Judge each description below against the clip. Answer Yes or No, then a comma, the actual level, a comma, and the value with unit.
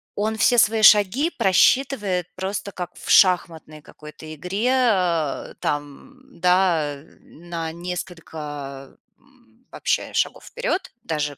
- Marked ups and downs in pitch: Yes, wide, 5.8 semitones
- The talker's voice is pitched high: No, medium, 180 Hz